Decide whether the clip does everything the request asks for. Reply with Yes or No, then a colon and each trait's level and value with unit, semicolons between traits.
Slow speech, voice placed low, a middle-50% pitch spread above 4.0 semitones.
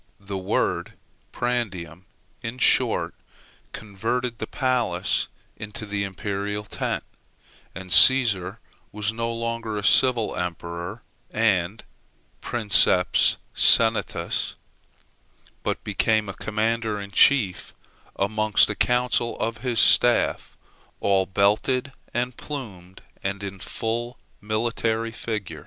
No: slow, 105 wpm; low, 110 Hz; average, 3.0 semitones